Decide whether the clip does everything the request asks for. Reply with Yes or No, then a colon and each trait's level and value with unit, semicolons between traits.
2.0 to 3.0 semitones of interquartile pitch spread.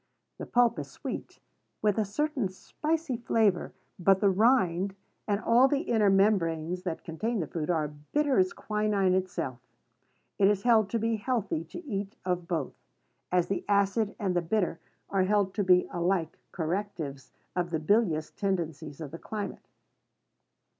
No: average, 3.9 semitones